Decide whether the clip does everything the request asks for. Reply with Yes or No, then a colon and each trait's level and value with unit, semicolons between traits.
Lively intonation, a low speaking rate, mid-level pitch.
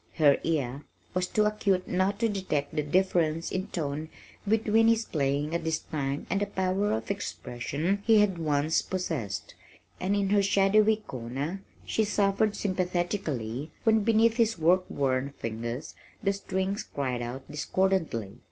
No: wide, 5.9 semitones; average, 150 wpm; medium, 180 Hz